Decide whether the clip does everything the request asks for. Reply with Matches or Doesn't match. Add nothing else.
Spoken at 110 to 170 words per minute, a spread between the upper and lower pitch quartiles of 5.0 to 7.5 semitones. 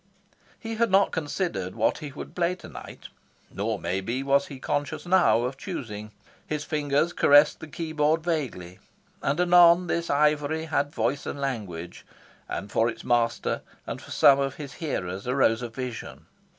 Matches